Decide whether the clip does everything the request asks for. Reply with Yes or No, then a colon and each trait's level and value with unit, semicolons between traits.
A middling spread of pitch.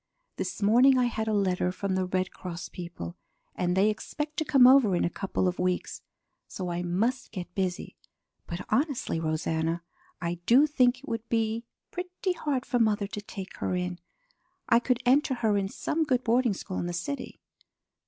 No: wide, 5.9 semitones